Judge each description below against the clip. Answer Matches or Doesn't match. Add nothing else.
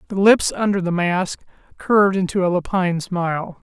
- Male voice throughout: Matches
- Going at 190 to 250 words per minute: Doesn't match